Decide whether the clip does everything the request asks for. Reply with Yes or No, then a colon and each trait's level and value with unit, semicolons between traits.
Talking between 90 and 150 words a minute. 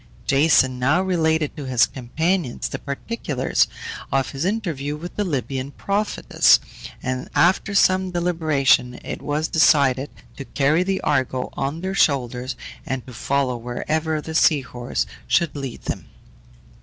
Yes: average, 140 wpm